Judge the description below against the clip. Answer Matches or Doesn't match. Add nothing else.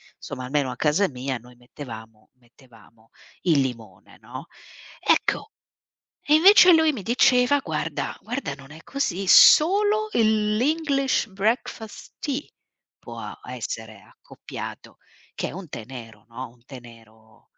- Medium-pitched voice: Matches